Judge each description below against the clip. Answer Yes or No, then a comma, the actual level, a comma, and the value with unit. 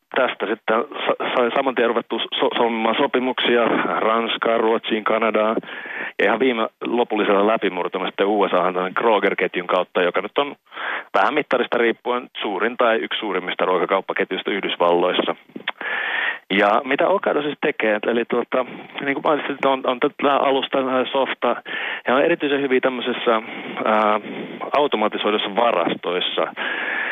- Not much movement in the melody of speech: No, average, 3.0 semitones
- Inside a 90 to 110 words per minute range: No, average, 125 wpm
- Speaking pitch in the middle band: No, low, 115 Hz